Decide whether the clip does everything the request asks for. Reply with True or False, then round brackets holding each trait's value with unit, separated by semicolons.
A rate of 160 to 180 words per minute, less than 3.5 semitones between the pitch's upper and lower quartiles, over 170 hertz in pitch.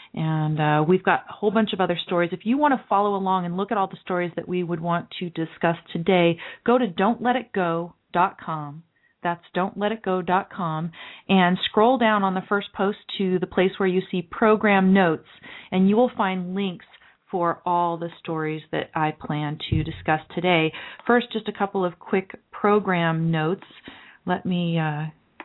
True (175 wpm; 2.9 semitones; 185 Hz)